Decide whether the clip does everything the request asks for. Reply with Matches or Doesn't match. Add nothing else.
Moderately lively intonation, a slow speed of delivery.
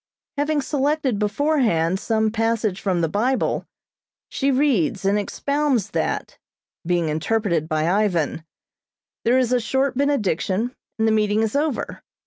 Doesn't match